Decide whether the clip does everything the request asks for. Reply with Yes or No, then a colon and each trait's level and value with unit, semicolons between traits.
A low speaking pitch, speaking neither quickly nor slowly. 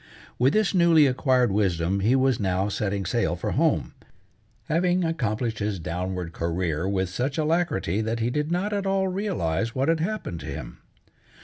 Yes: low, 115 Hz; average, 170 wpm